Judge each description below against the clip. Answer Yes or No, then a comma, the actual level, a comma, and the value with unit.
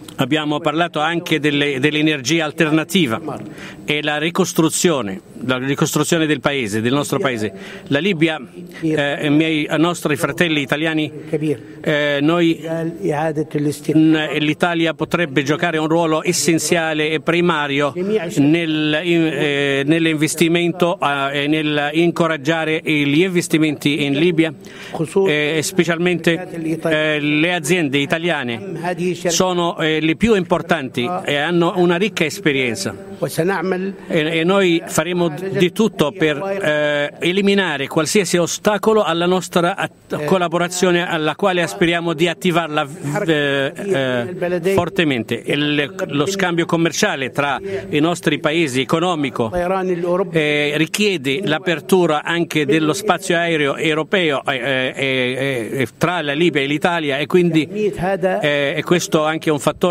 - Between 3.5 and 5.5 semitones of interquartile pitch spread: No, average, 2.8 semitones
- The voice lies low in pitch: No, medium, 160 Hz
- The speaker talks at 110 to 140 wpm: Yes, average, 120 wpm